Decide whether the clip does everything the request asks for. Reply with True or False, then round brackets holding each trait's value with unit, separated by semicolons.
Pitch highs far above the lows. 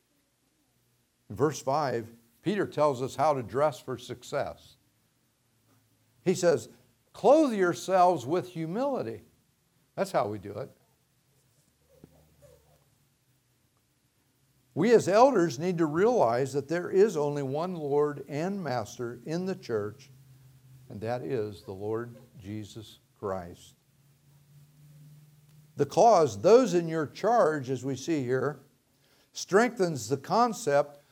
False (4.6 semitones)